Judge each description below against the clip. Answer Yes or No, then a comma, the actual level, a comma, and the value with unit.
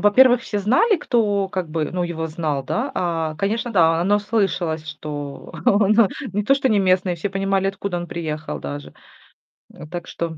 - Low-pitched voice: No, medium, 185 Hz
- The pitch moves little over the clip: No, average, 4.3 semitones